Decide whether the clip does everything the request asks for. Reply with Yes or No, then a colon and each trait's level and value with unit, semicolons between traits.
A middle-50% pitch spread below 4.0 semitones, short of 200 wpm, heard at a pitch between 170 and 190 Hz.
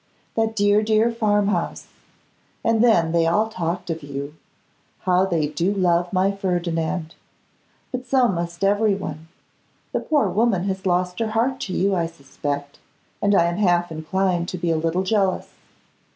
Yes: average, 3.5 semitones; average, 160 wpm; medium, 185 Hz